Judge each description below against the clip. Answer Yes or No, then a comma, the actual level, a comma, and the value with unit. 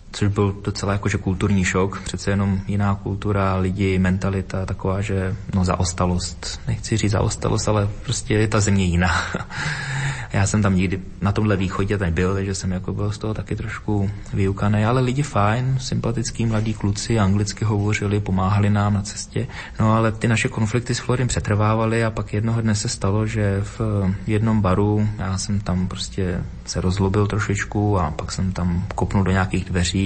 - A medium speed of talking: No, fast, 175 wpm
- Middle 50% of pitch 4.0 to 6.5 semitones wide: No, narrow, 2.4 semitones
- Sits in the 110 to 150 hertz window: No, low, 100 Hz